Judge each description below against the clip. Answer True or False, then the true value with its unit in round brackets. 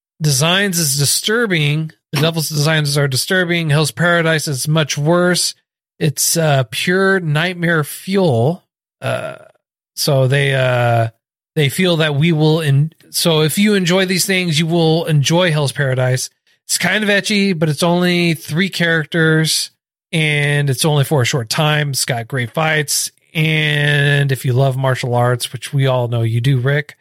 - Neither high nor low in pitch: True (155 Hz)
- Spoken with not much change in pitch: False (3.5 semitones)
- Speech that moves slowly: False (160 wpm)